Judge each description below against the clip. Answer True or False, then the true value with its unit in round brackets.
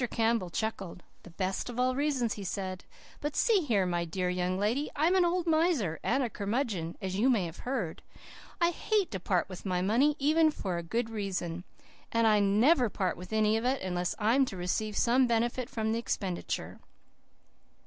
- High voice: True (220 Hz)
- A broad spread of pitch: True (5.9 semitones)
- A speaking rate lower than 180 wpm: False (190 wpm)